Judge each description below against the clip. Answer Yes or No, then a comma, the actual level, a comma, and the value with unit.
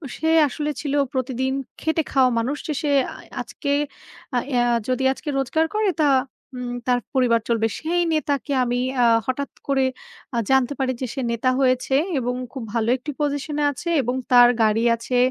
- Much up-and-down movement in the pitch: No, average, 2.7 semitones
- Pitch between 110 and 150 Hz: No, very high, 265 Hz